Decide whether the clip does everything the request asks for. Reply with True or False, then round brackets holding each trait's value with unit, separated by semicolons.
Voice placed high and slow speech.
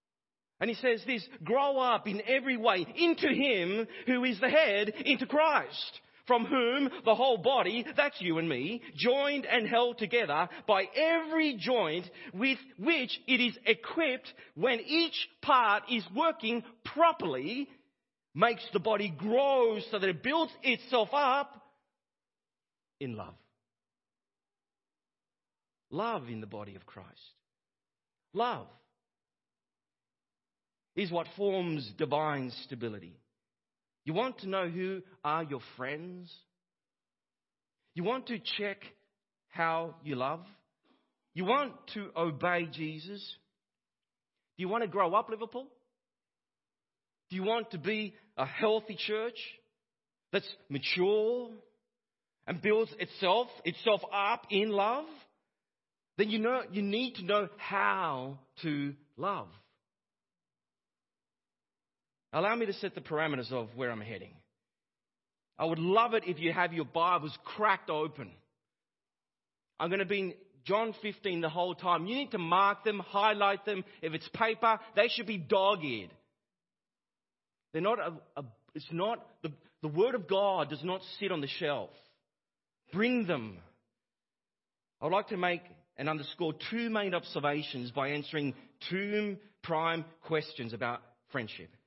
True (205 Hz; 130 wpm)